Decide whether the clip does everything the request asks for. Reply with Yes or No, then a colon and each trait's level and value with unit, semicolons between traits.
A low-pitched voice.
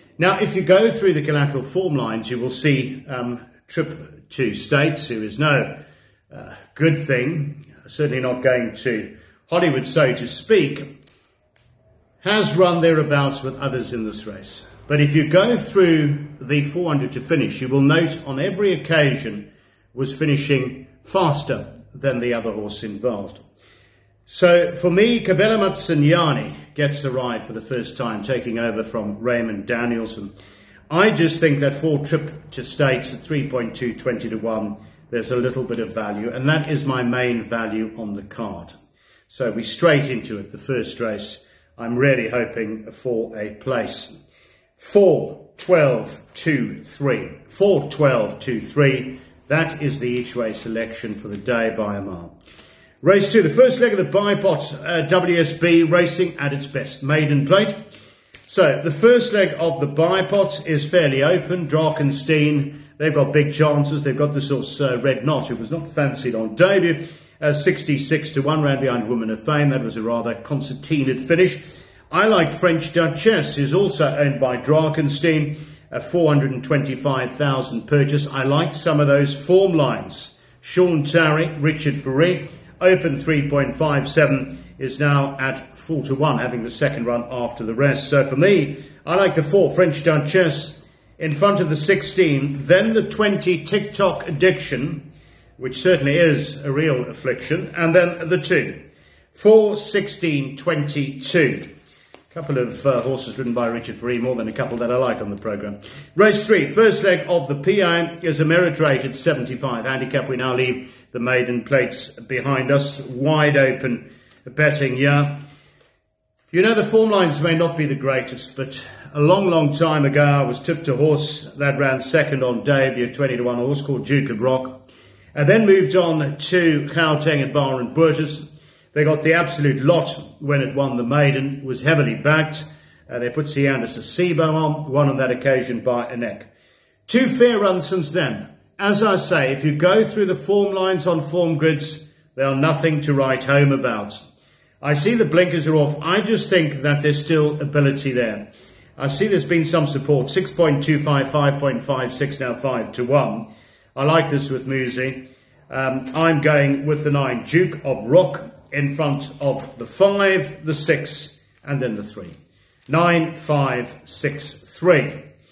No: medium, 145 Hz